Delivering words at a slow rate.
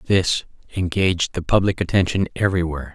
Yes: slow, 120 wpm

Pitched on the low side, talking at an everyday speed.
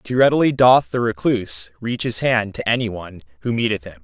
No: low, 110 Hz; fast, 210 wpm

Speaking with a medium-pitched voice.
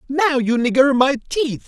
No: very high, 265 Hz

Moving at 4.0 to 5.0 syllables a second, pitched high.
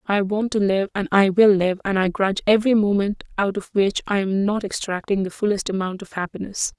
No: 5.6 syllables/s; high, 200 Hz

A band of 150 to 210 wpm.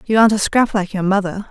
No: fast, 280 wpm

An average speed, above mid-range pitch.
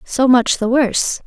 Yes: average, 190 wpm; high, 245 Hz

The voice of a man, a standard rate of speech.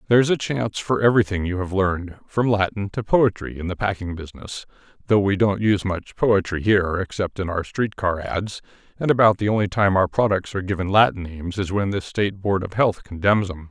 No: male; fast, 215 wpm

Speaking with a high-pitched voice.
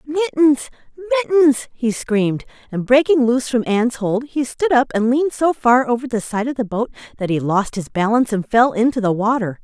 Yes: high, 245 Hz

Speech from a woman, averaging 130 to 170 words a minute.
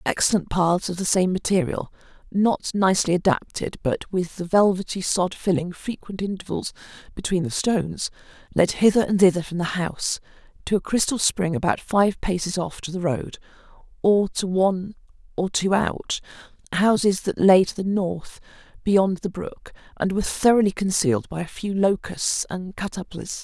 Yes: female; average, 160 wpm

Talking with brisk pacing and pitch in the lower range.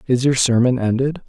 No: average, 190 wpm; low, 125 Hz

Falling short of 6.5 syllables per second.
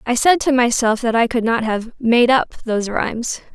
Yes: 4.9 syllables/s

